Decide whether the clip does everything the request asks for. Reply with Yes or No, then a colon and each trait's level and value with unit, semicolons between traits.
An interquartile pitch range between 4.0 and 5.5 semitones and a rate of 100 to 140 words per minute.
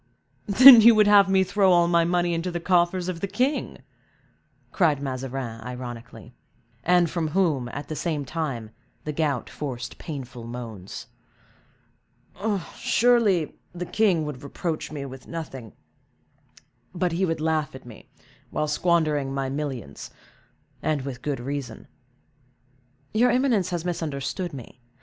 Yes: average, 5.1 semitones; slow, 135 wpm